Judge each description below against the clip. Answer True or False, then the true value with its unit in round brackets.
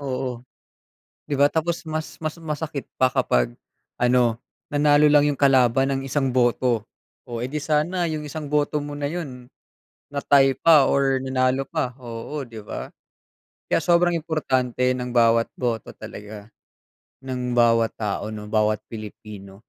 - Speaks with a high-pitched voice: False (130 Hz)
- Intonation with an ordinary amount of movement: True (3.9 semitones)